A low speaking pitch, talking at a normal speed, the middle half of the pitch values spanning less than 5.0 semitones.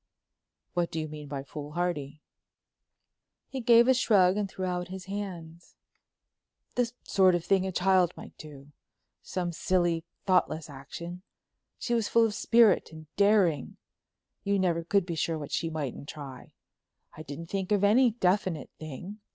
No: medium, 180 Hz; average, 155 wpm; average, 4.1 semitones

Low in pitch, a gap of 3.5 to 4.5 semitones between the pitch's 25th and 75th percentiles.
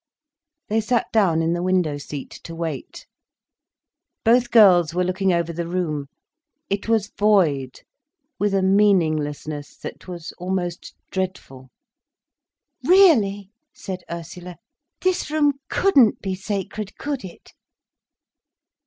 No: medium, 185 Hz; average, 3.9 semitones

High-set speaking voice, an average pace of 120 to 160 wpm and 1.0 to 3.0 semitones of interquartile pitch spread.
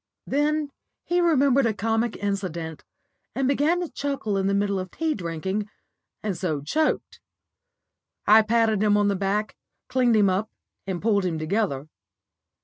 No: high, 210 Hz; average, 150 wpm; wide, 5.4 semitones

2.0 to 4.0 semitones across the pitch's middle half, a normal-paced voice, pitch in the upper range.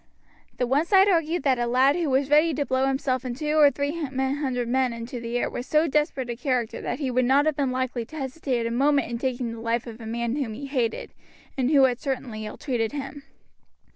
No: average, 3.1 semitones; fast, 235 wpm; very high, 260 Hz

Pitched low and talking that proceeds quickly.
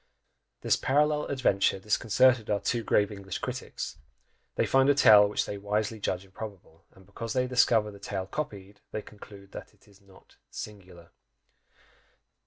No: low, 105 Hz; average, 155 wpm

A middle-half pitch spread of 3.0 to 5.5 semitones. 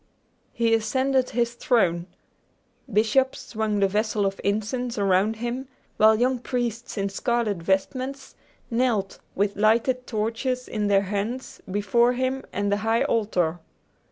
Yes: average, 3.4 semitones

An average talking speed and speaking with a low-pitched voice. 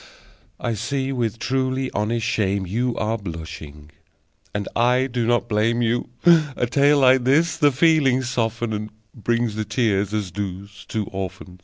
Yes: average, 155 wpm; low, 115 Hz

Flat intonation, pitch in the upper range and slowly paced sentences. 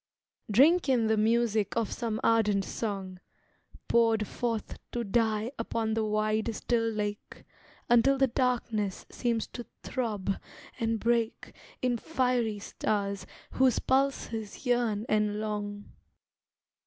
Yes: narrow, 2.1 semitones; high, 225 Hz; slow, 115 wpm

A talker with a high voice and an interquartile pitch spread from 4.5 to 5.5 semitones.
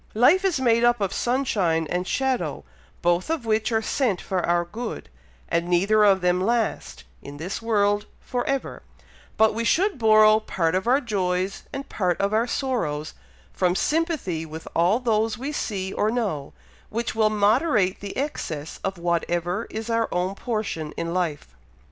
Yes: high, 210 Hz; average, 4.9 semitones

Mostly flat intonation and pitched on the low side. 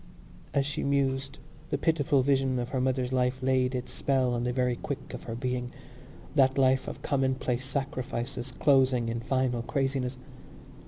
Yes: narrow, 1.4 semitones; low, 130 Hz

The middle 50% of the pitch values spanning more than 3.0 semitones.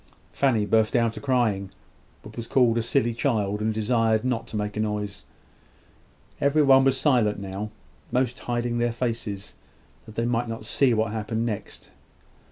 No: narrow, 2.4 semitones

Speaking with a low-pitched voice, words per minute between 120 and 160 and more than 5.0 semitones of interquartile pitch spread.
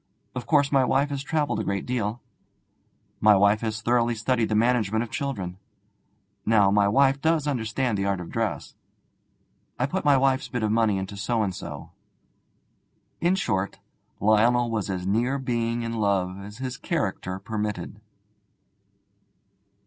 No: low, 115 Hz; average, 155 wpm; average, 4.2 semitones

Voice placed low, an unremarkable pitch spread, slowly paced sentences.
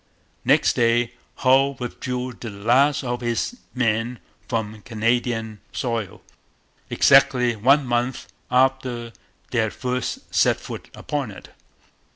No: low, 120 Hz; narrow, 1.9 semitones; slow, 115 wpm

